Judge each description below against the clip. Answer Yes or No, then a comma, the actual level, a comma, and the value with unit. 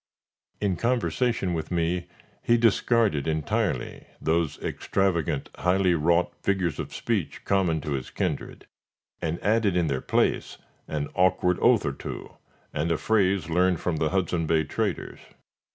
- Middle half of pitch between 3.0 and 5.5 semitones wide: Yes, average, 3.5 semitones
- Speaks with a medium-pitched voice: No, very low, 90 Hz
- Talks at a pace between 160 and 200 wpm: No, average, 140 wpm